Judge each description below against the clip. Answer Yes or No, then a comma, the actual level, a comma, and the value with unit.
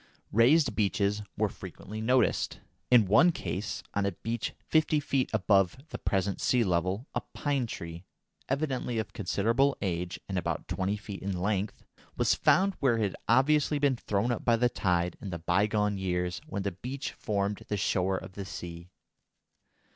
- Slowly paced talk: No, average, 170 wpm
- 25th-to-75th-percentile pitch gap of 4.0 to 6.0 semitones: Yes, average, 4.6 semitones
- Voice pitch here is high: No, low, 105 Hz